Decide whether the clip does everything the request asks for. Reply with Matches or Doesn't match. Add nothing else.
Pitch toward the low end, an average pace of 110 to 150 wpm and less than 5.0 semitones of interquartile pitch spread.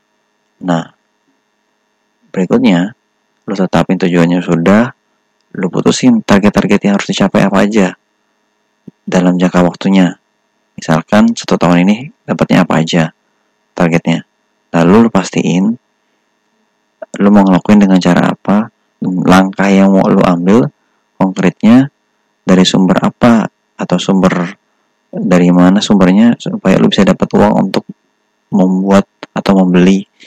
Matches